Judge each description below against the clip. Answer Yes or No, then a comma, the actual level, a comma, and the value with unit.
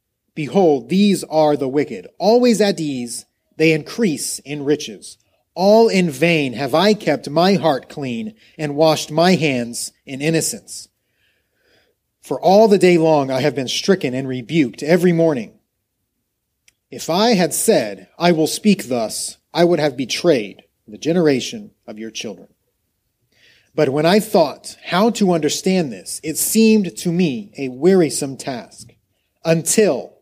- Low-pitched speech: No, medium, 160 Hz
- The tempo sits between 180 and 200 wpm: No, average, 145 wpm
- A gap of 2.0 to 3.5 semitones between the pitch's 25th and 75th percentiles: No, average, 5.3 semitones